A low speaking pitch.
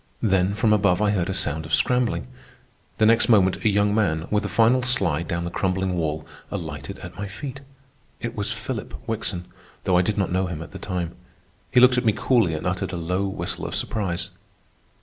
Yes: very low, 95 Hz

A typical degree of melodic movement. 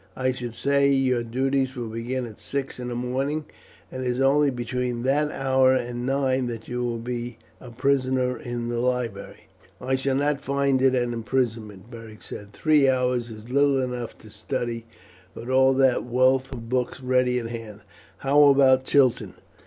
No: narrow, 1.9 semitones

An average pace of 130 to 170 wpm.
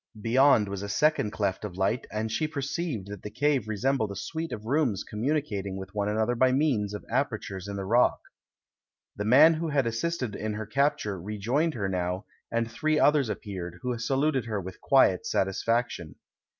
No: average, 185 wpm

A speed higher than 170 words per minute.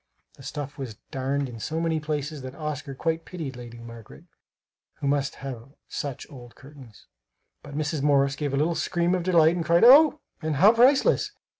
Yes: average, 180 wpm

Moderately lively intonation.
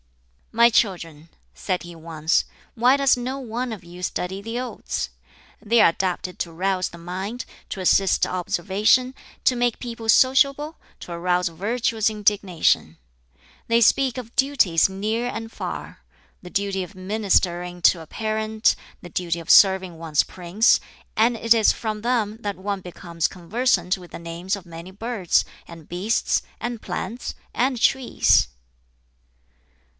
Yes: average, 4.7 semitones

